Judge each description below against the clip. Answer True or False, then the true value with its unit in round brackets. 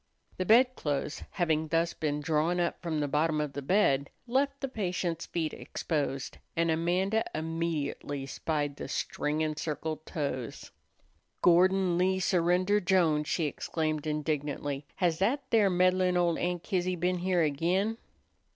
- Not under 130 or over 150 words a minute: True (140 wpm)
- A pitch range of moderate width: True (3.4 semitones)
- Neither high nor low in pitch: True (170 Hz)